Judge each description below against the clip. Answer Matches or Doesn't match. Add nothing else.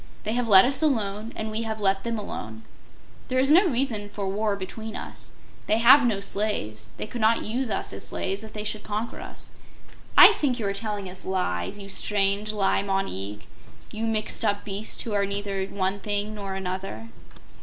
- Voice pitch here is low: Doesn't match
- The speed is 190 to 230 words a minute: Matches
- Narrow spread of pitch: Matches